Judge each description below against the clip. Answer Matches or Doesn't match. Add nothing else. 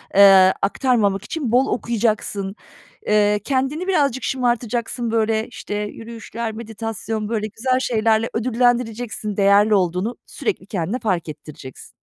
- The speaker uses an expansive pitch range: Doesn't match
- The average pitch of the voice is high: Matches